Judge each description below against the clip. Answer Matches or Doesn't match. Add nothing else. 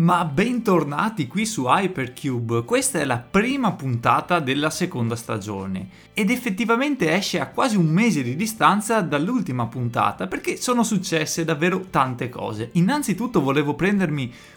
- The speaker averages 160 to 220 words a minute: Doesn't match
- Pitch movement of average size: Doesn't match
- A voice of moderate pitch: Matches